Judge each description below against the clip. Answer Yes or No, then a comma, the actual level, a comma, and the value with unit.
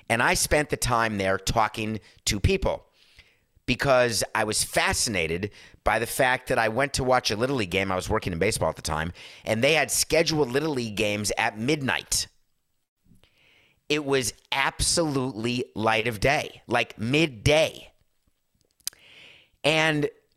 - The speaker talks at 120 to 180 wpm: Yes, average, 150 wpm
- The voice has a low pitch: Yes, low, 115 Hz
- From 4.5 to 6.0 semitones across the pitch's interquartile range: Yes, average, 4.8 semitones